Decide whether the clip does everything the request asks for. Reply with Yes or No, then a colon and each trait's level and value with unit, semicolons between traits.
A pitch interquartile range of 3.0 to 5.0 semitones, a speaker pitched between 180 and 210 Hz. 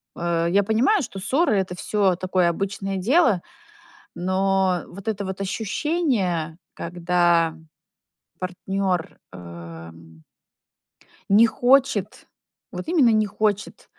Yes: average, 3.7 semitones; high, 190 Hz